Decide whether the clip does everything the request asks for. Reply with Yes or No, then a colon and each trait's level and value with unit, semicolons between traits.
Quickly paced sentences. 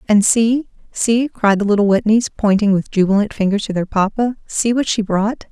No: average, 185 wpm